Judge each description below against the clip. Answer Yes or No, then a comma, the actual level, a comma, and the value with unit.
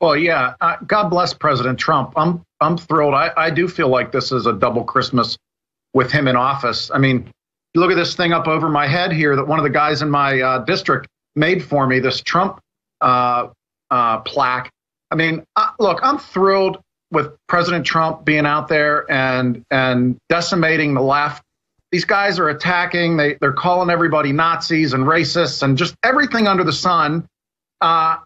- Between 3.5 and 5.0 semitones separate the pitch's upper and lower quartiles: Yes, average, 4.3 semitones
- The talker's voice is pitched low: No, medium, 155 Hz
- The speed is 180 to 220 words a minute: Yes, average, 185 wpm